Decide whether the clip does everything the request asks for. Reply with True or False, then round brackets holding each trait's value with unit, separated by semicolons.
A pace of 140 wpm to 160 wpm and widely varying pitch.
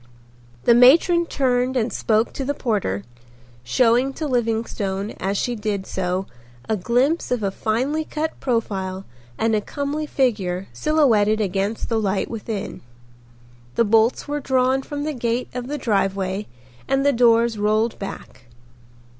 False (145 wpm; 4.3 semitones)